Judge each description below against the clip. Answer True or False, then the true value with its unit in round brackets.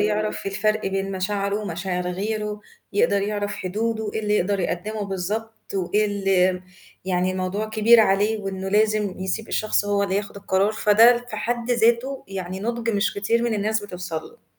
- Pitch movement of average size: False (2.2 semitones)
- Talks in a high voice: True (205 Hz)